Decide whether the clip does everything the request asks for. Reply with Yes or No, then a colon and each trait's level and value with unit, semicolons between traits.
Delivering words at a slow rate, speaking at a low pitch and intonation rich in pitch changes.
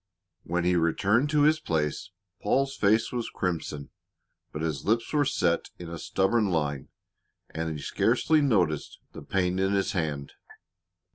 No: average, 150 wpm; very low, 90 Hz; wide, 6.1 semitones